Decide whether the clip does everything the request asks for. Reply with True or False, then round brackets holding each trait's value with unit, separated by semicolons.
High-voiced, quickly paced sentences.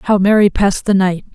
True (195 Hz; 225 wpm)